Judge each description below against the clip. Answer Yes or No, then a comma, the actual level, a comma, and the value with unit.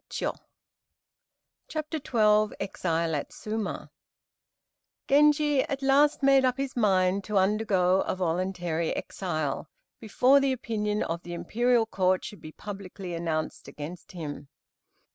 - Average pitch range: No, wide, 6.3 semitones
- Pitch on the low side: No, high, 200 Hz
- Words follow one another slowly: Yes, slow, 125 wpm